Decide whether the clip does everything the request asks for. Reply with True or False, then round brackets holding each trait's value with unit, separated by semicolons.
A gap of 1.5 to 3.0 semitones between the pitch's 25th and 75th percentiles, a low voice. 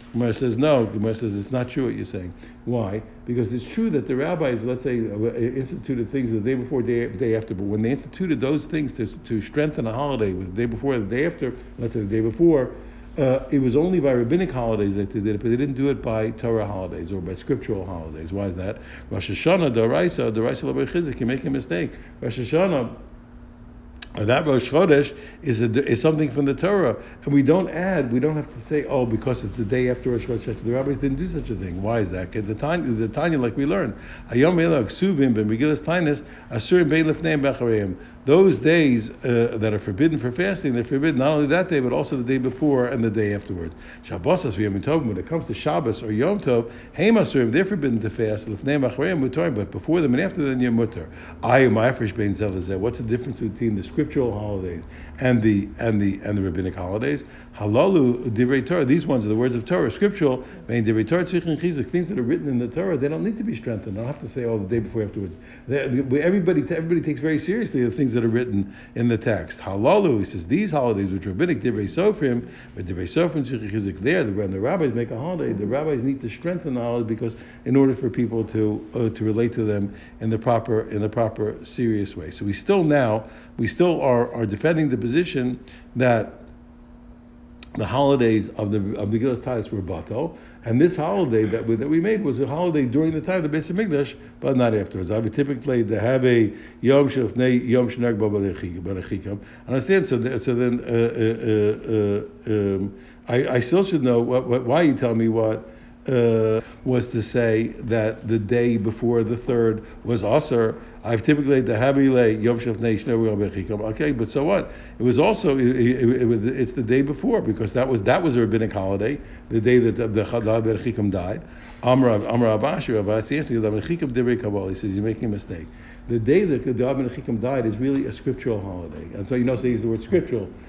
False (4.1 semitones; 120 Hz)